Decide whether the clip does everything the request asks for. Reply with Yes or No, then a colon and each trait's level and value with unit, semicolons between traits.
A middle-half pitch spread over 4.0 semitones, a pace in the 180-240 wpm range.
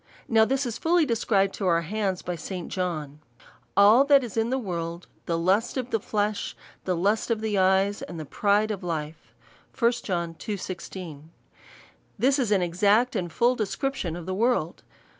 Yes: average, 4.6 semitones; average, 185 wpm